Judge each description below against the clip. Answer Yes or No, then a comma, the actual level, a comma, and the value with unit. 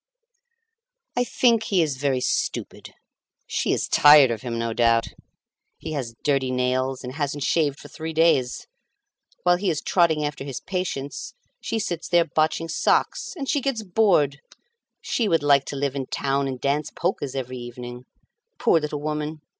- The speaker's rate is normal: Yes, average, 165 wpm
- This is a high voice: No, medium, 145 Hz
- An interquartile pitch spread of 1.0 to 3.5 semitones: No, average, 4.1 semitones